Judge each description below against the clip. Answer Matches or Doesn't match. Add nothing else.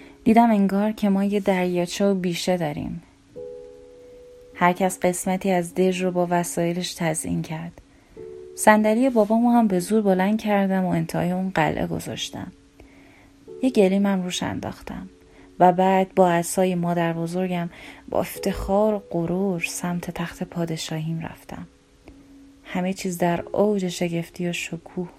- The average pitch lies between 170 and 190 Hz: Matches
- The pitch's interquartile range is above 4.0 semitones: Doesn't match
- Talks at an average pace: Matches